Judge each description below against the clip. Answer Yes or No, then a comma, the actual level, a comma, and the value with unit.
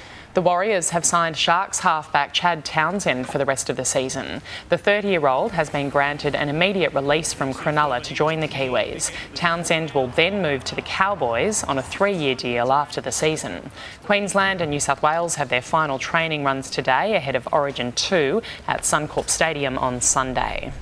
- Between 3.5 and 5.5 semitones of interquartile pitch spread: Yes, average, 3.9 semitones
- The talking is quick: No, average, 185 wpm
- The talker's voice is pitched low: No, medium, 150 Hz